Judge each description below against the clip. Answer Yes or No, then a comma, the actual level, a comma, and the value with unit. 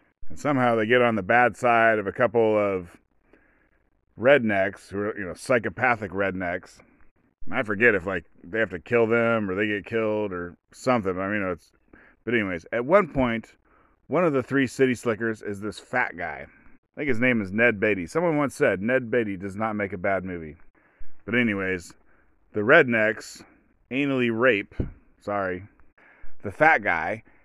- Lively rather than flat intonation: No, average, 3.7 semitones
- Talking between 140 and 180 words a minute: Yes, average, 175 wpm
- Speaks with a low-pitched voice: Yes, low, 110 Hz